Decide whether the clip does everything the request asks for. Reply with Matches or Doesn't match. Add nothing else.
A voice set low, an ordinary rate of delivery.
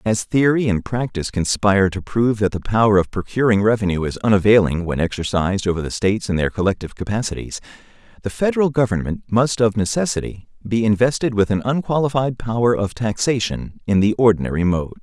Matches